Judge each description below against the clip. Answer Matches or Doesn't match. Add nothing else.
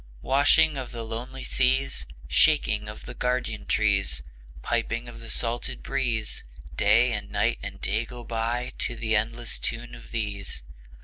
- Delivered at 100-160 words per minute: Matches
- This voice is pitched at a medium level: Doesn't match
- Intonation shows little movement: Matches